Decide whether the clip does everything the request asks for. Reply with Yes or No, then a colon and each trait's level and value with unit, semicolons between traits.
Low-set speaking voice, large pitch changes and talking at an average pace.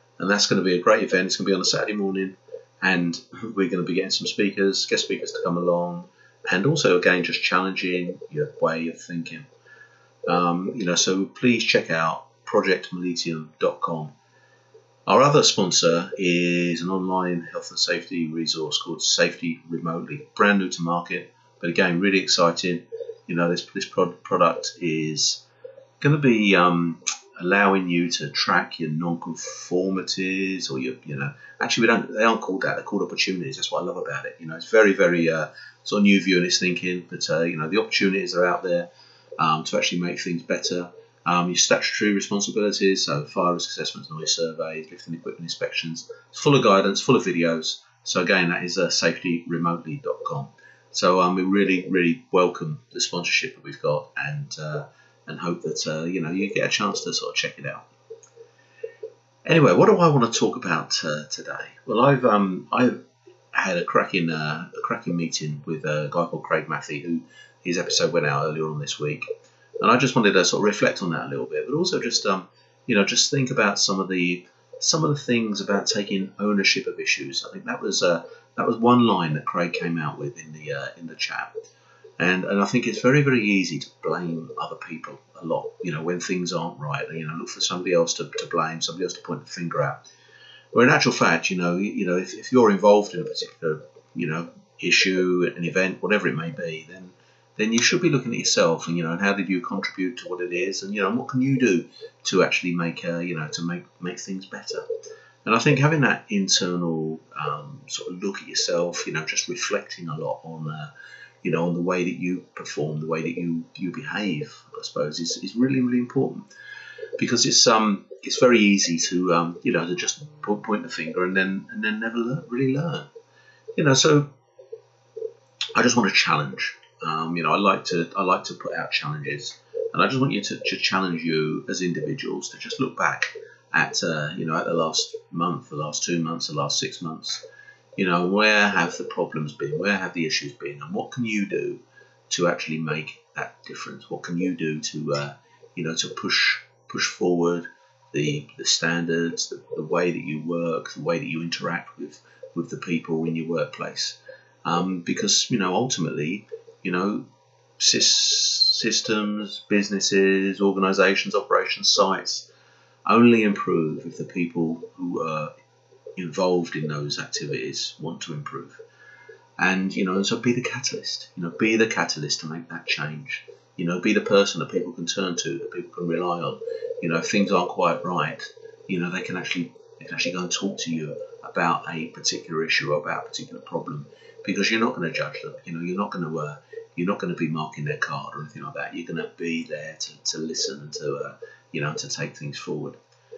No: very low, 90 Hz; wide, 6.1 semitones; fast, 210 wpm